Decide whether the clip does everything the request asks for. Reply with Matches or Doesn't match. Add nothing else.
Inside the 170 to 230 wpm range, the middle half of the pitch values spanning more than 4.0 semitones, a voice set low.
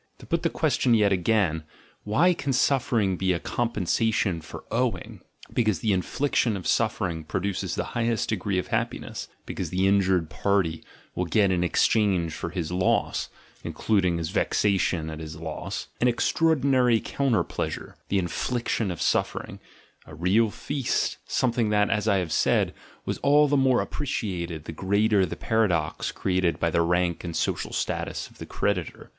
Matches